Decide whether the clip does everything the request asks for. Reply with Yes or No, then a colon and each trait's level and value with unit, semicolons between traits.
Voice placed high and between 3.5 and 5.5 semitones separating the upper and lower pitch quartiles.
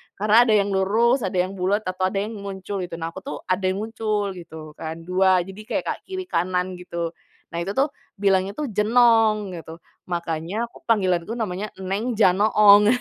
No: high, 195 Hz; average, 2.9 semitones